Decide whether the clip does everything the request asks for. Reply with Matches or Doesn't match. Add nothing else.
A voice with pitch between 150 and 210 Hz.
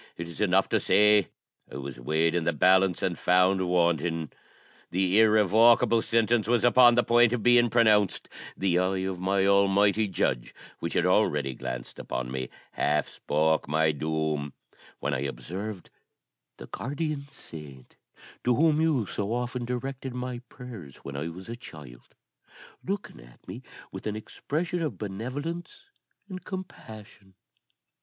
Doesn't match